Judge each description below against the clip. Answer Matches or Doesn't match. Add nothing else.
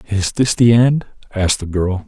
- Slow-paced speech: Doesn't match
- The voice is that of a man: Matches